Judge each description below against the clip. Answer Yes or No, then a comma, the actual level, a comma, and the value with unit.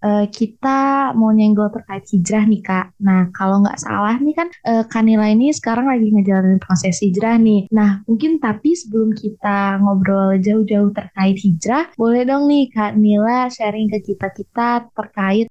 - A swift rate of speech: Yes, fast, 165 wpm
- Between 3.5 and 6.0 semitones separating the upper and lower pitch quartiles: No, narrow, 2.5 semitones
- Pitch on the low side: No, high, 215 Hz